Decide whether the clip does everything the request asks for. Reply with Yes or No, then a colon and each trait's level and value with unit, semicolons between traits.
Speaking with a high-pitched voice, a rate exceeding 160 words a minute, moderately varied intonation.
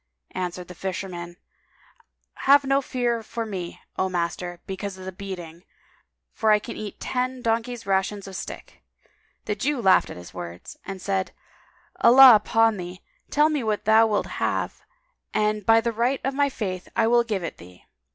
Yes: high, 210 Hz; average, 170 wpm; average, 4.2 semitones